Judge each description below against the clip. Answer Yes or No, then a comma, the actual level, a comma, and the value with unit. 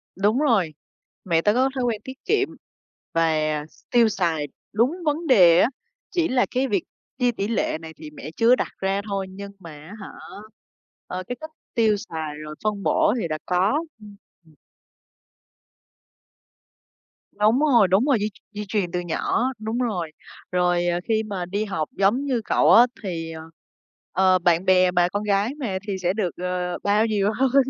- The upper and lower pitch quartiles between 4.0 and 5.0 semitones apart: Yes, average, 4.7 semitones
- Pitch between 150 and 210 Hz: Yes, high, 200 Hz